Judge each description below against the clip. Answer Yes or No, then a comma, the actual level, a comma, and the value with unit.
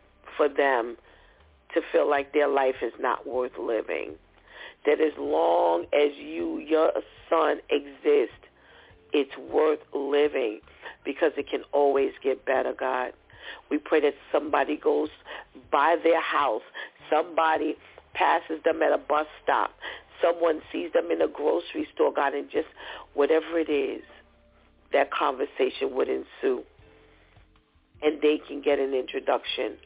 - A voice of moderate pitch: No, very high, 310 Hz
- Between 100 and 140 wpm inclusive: Yes, slow, 135 wpm